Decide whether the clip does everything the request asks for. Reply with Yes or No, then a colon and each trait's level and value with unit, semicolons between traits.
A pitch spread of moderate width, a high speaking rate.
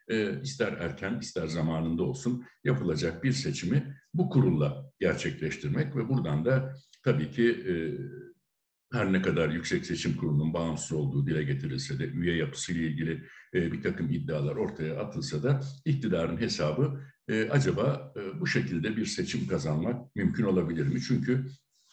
No: wide, 8.9 semitones; fast, 145 wpm